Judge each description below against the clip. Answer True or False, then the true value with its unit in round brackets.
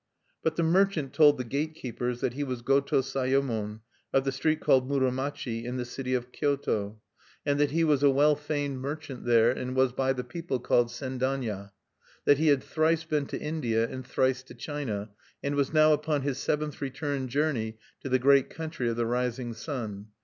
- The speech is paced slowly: False (190 wpm)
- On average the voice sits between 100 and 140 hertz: True (135 Hz)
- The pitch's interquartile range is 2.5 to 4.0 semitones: True (3.0 semitones)